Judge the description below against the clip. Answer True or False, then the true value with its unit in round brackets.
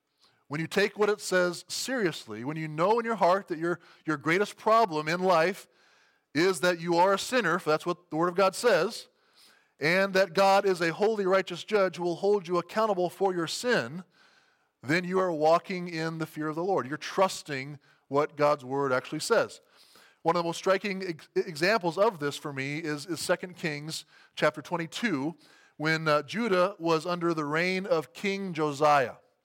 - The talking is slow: False (190 wpm)